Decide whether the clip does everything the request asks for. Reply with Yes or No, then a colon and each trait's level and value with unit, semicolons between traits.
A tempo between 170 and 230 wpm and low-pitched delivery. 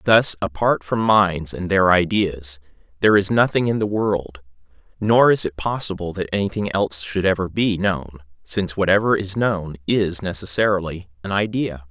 No: average, 160 wpm; very low, 95 Hz